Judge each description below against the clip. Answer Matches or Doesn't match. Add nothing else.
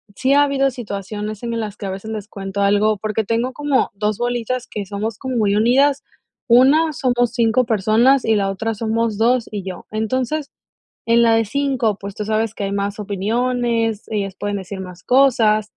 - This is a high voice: Matches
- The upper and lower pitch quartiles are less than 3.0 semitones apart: Doesn't match